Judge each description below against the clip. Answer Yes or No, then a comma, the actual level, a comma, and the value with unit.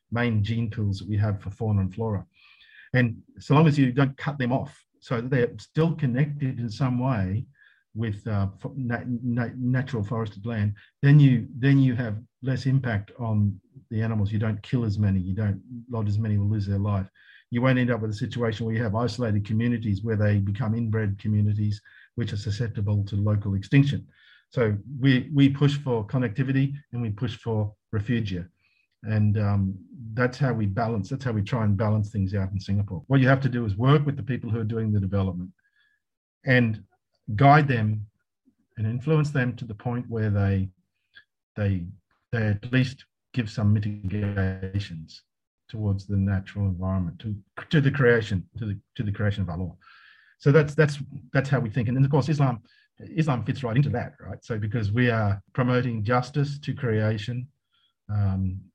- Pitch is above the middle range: No, low, 115 Hz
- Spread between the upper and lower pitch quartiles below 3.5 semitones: No, average, 3.8 semitones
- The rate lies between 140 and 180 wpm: No, average, 190 wpm